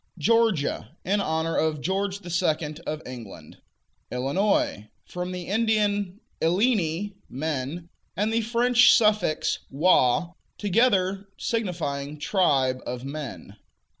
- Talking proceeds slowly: Yes, slow, 105 wpm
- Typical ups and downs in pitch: No, wide, 5.9 semitones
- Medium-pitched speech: Yes, medium, 180 Hz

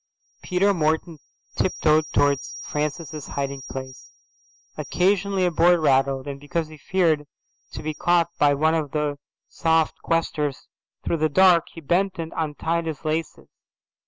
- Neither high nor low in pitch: Yes, medium, 160 Hz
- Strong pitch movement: No, average, 2.7 semitones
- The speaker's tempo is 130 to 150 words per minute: Yes, average, 140 wpm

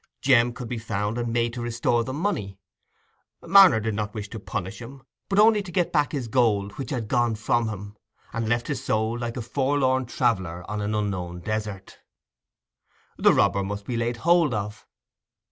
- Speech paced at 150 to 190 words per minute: Yes, average, 185 wpm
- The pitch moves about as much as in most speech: Yes, average, 3.5 semitones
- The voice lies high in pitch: No, low, 115 Hz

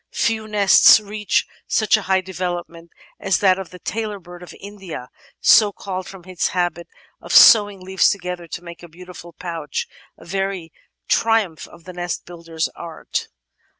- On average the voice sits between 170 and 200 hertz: Yes, medium, 185 Hz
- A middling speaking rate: Yes, average, 160 wpm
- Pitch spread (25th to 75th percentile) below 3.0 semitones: Yes, narrow, 2.6 semitones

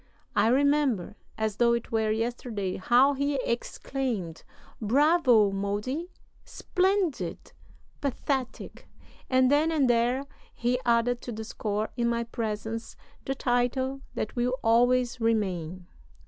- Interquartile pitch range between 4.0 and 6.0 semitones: No, average, 3.4 semitones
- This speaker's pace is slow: Yes, slow, 120 wpm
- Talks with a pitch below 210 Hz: No, high, 240 Hz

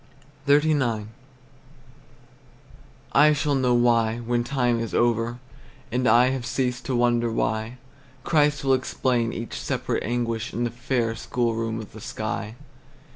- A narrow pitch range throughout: Yes, narrow, 2.1 semitones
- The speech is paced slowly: Yes, slow, 130 wpm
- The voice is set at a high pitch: No, low, 120 Hz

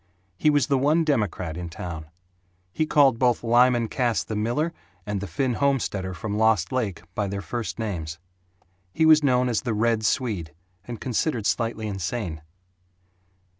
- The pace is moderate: Yes, average, 160 wpm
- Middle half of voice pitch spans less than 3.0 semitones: No, average, 4.7 semitones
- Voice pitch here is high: No, low, 115 Hz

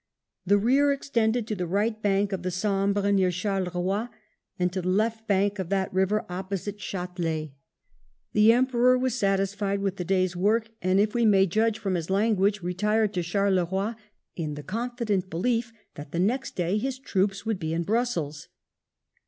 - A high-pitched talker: Yes, high, 200 Hz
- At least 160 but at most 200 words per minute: Yes, average, 170 wpm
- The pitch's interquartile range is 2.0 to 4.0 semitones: Yes, average, 3.1 semitones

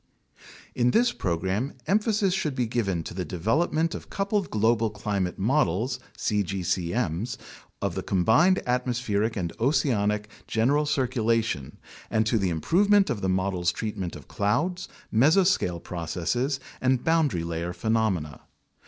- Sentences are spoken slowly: Yes, slow, 125 wpm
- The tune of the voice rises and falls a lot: Yes, wide, 6.9 semitones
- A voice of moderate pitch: No, low, 110 Hz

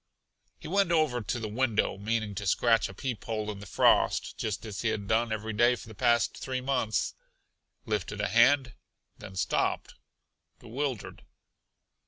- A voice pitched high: No, low, 115 Hz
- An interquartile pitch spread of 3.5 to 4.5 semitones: No, average, 2.8 semitones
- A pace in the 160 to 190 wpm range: Yes, average, 165 wpm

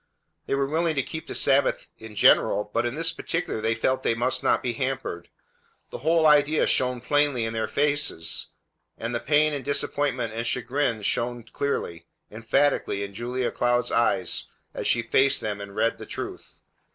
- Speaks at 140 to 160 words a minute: No, average, 175 wpm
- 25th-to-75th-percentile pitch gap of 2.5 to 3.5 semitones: No, average, 4.1 semitones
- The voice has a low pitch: Yes, low, 125 Hz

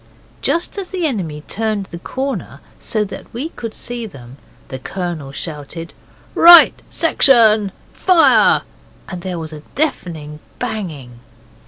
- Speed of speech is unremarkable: No, slow, 130 wpm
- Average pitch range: No, wide, 8.0 semitones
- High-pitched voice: Yes, high, 195 Hz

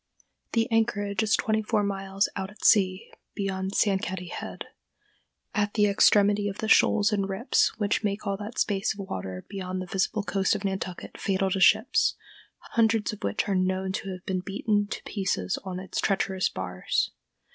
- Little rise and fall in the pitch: Yes, narrow, 1.6 semitones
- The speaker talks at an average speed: Yes, average, 175 wpm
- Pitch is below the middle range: No, high, 195 Hz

